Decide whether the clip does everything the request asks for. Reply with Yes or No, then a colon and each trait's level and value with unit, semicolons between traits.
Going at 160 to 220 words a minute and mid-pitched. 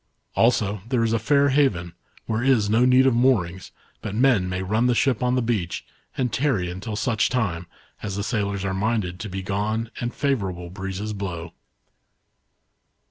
No: average, 175 wpm; low, 110 Hz